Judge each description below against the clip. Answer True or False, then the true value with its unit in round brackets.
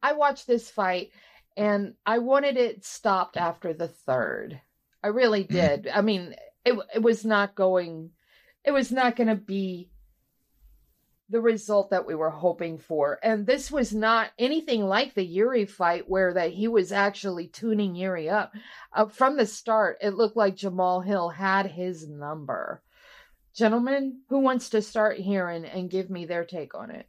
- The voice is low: False (205 Hz)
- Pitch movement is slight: False (4.2 semitones)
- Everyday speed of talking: True (175 wpm)